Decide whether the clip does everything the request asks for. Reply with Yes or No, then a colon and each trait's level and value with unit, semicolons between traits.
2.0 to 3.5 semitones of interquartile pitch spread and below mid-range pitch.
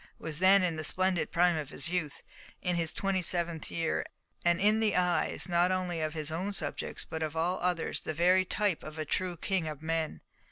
No: narrow, 2.5 semitones; medium, 175 Hz